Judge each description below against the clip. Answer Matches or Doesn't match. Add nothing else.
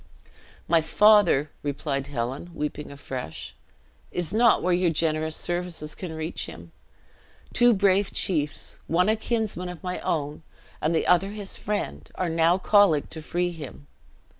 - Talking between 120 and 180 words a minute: Matches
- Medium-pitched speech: Matches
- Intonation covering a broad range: Doesn't match